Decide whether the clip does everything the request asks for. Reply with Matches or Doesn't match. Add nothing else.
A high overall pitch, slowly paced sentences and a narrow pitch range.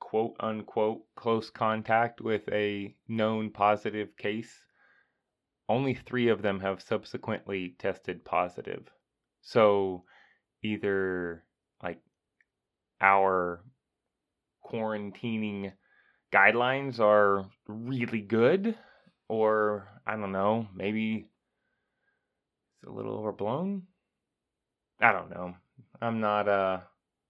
Doesn't match